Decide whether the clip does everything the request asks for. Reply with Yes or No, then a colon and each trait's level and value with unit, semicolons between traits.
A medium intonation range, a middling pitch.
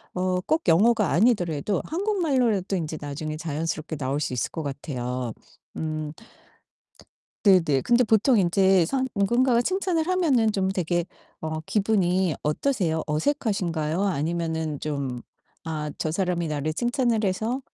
No: wide, 6.5 semitones; medium, 180 Hz